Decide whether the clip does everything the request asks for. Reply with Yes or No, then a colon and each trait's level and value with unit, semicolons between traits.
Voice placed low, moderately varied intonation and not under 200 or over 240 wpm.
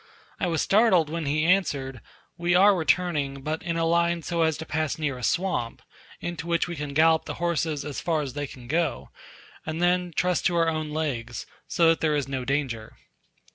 No: medium, 160 Hz; average, 3.1 semitones; fast, 205 wpm